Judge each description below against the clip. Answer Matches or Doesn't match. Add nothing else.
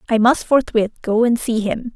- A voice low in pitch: Doesn't match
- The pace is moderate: Doesn't match